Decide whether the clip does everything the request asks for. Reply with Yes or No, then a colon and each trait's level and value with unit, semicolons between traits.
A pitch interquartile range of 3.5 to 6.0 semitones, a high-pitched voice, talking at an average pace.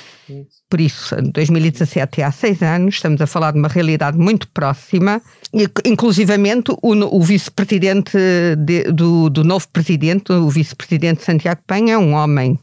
No: average, 4.2 semitones; medium, 170 Hz; average, 150 wpm